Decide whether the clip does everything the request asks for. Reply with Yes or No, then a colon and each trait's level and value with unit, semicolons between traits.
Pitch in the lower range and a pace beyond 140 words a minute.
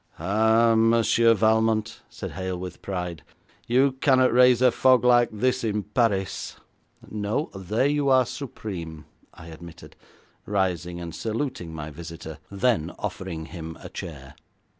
No: low, 105 Hz; slow, 135 wpm